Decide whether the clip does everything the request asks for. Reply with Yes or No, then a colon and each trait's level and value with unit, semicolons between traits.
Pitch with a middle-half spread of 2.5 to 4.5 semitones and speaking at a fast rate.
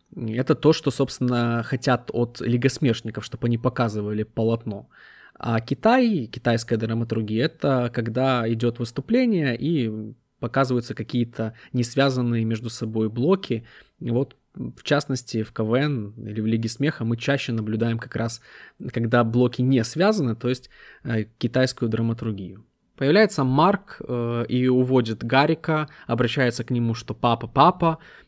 No: average, 2.9 semitones; average, 125 wpm